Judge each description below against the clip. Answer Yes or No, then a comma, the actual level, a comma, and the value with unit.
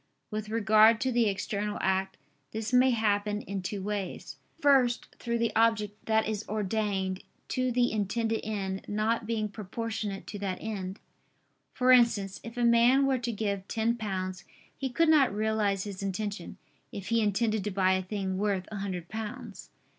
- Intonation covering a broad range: No, average, 2.7 semitones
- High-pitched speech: Yes, high, 215 Hz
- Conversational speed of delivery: Yes, average, 170 wpm